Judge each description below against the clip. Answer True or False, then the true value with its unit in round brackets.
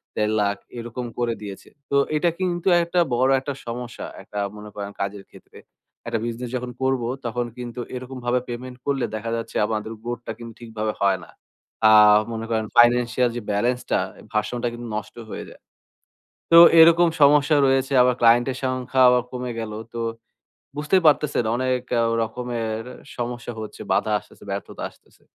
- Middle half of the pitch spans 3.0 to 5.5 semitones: False (2.4 semitones)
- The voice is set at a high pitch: False (120 Hz)